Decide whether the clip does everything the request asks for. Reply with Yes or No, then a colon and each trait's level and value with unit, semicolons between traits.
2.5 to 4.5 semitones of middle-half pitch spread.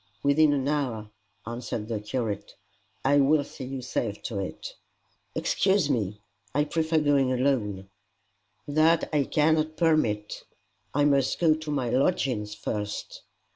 No: wide, 5.6 semitones